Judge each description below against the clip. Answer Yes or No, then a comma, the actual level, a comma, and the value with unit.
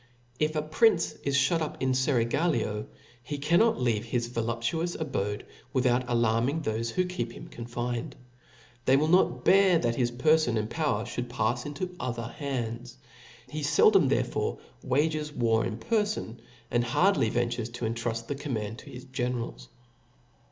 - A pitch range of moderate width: Yes, average, 4.7 semitones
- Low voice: Yes, low, 125 Hz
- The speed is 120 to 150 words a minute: No, average, 160 wpm